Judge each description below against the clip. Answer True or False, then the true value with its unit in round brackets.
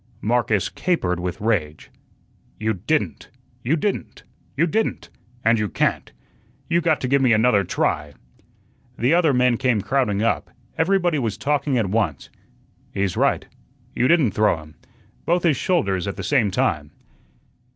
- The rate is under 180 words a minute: True (150 wpm)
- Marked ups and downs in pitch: True (7.2 semitones)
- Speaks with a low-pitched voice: True (120 Hz)